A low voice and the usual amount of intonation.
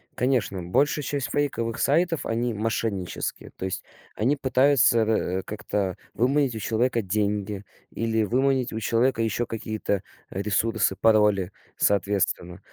Yes: low, 110 Hz; average, 3.8 semitones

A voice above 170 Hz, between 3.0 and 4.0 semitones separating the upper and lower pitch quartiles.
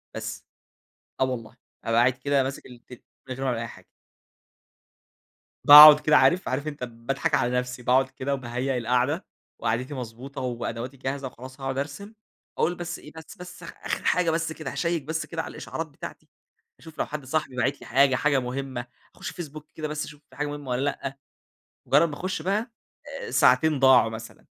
No: low, 135 Hz; average, 3.4 semitones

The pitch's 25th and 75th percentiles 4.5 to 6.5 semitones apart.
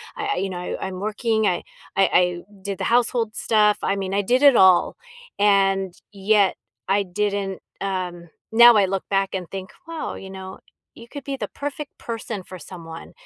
No: average, 2.9 semitones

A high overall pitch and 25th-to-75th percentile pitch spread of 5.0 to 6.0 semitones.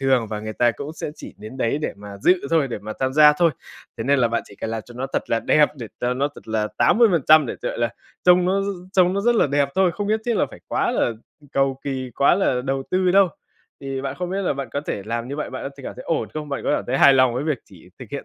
No: low, 135 Hz; average, 5.3 semitones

